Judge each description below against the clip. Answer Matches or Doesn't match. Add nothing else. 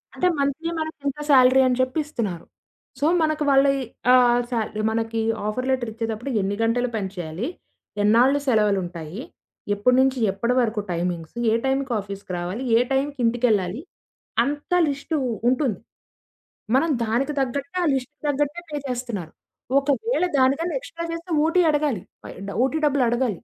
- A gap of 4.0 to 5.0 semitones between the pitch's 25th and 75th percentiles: Matches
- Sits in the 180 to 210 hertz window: Doesn't match